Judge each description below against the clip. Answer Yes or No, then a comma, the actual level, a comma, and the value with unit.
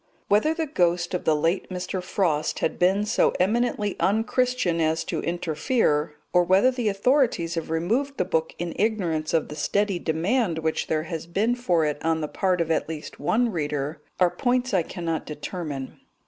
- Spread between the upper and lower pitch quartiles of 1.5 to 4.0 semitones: No, average, 4.9 semitones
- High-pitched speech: No, medium, 175 Hz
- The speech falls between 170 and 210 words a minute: Yes, average, 180 wpm